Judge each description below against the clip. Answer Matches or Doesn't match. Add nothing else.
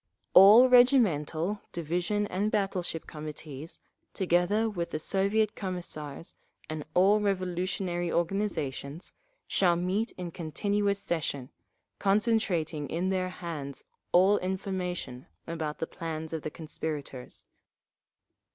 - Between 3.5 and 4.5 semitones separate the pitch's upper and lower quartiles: Matches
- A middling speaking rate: Doesn't match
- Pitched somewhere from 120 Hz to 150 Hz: Doesn't match